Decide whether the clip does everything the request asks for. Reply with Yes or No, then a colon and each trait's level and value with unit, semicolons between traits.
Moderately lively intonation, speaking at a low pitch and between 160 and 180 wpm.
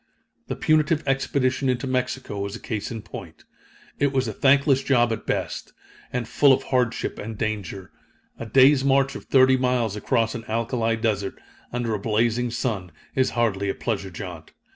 Yes: average, 3.4 semitones; low, 120 Hz; average, 170 wpm